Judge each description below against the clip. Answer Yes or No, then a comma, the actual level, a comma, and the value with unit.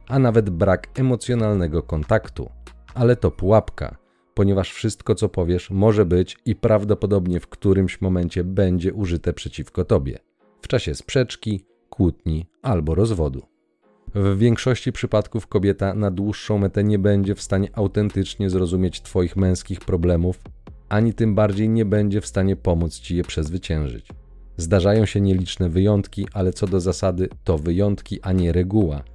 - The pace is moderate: Yes, average, 140 wpm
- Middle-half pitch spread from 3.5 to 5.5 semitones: No, average, 2.8 semitones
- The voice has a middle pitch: No, very low, 95 Hz